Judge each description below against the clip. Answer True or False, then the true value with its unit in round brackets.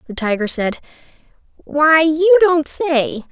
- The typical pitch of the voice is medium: False (295 Hz)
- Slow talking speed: True (125 wpm)